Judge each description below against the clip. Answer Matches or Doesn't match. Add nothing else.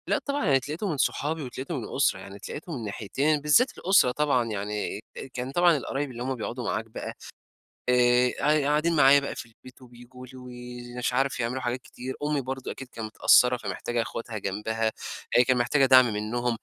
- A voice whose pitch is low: Matches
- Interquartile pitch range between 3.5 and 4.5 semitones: Doesn't match